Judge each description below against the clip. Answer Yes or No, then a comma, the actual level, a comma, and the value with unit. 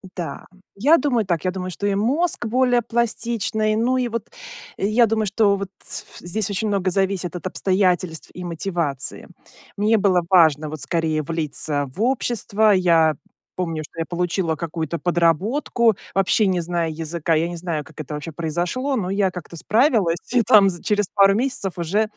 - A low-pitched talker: No, medium, 185 Hz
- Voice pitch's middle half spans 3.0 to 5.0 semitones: Yes, average, 4.6 semitones